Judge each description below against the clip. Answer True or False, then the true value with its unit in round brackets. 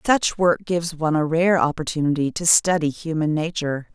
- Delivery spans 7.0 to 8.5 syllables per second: False (5.5 syllables/s)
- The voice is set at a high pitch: False (160 Hz)